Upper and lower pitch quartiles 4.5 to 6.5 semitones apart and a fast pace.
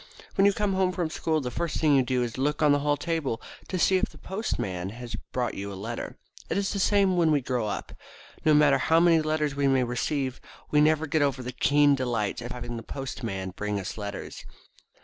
Yes: average, 4.8 semitones; fast, 230 wpm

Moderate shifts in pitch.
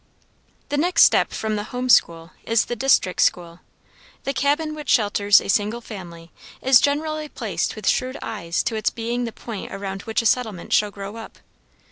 Yes: average, 4.5 semitones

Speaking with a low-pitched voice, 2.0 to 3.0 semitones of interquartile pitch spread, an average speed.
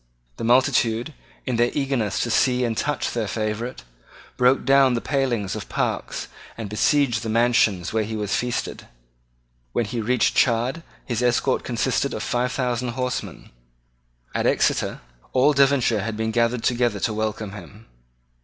Yes: low, 120 Hz; narrow, 2.5 semitones; average, 155 wpm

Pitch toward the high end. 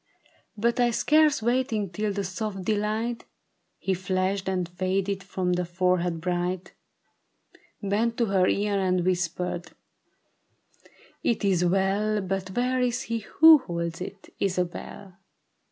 Yes: high, 195 Hz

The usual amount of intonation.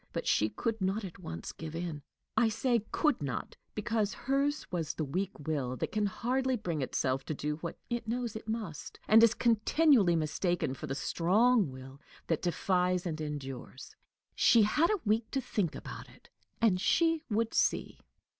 No: wide, 6.9 semitones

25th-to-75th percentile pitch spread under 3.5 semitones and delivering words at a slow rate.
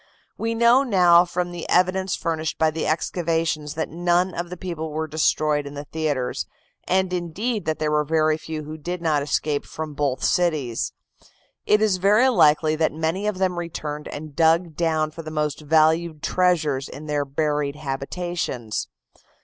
No: average, 2.8 semitones; average, 170 wpm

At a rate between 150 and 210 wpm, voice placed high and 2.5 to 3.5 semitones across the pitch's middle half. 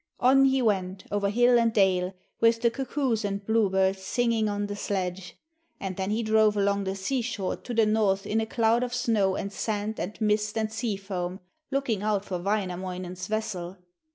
Yes: average, 185 wpm; high, 210 Hz; average, 2.9 semitones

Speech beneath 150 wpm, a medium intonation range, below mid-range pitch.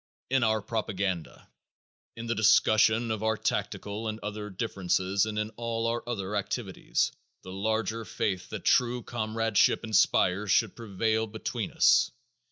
No: average, 140 wpm; narrow, 2.1 semitones; low, 110 Hz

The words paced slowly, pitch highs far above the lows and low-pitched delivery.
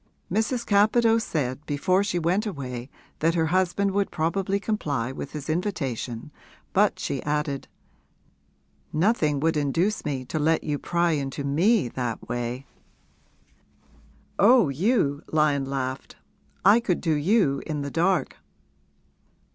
No: slow, 130 wpm; wide, 5.9 semitones; medium, 155 Hz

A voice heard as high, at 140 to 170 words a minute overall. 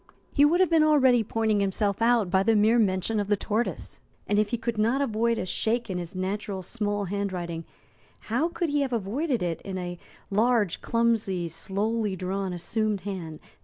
No: high, 210 Hz; average, 185 wpm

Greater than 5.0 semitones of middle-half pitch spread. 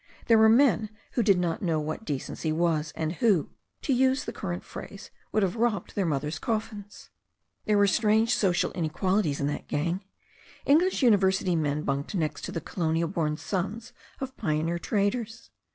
Yes: wide, 5.4 semitones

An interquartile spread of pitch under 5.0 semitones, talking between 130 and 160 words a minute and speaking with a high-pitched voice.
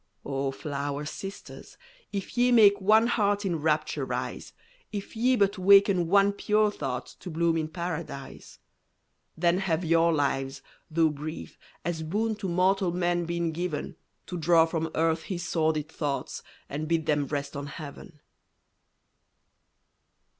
No: average, 4.2 semitones; average, 140 wpm; medium, 170 Hz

